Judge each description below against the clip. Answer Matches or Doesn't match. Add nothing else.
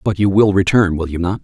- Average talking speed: Doesn't match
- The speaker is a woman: Doesn't match